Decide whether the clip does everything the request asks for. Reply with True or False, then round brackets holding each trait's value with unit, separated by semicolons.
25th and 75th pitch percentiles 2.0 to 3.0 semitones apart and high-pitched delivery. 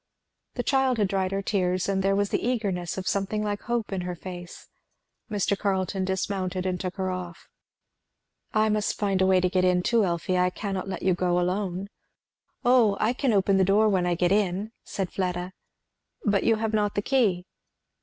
True (2.4 semitones; 195 Hz)